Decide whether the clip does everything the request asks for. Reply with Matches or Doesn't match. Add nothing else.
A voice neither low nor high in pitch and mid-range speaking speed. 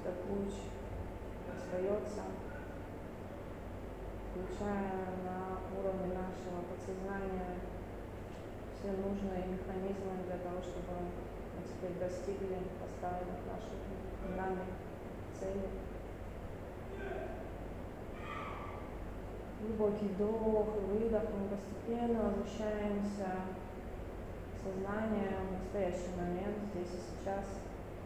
Doesn't match